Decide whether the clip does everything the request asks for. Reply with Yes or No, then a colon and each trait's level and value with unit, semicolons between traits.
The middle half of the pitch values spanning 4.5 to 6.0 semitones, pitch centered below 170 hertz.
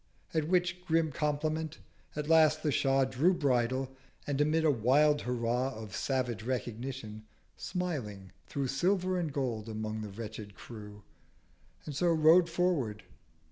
Yes: wide, 5.5 semitones; low, 135 Hz